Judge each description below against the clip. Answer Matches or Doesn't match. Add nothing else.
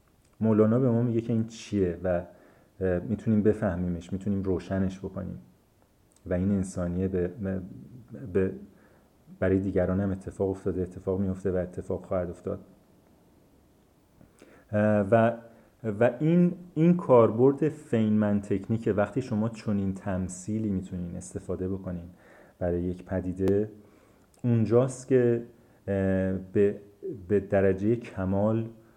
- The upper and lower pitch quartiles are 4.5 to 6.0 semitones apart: Doesn't match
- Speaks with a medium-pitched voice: Doesn't match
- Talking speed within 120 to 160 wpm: Doesn't match